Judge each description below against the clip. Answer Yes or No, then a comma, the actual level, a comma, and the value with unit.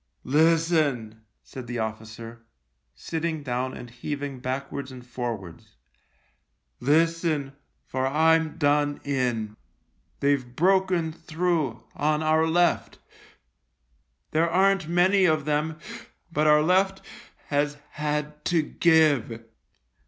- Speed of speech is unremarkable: No, slow, 110 wpm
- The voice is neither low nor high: Yes, medium, 150 Hz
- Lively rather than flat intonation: No, average, 4.2 semitones